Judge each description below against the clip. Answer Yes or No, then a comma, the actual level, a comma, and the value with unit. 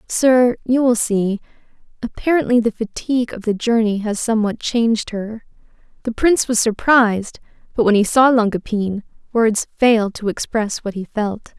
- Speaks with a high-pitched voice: Yes, high, 225 Hz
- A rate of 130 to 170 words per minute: Yes, average, 160 wpm